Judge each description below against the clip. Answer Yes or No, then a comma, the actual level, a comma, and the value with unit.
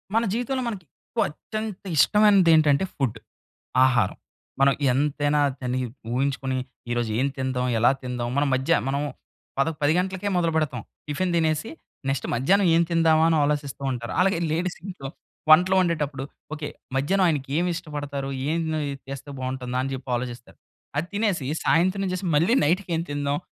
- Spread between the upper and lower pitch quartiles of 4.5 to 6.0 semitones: Yes, average, 4.9 semitones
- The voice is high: No, medium, 150 Hz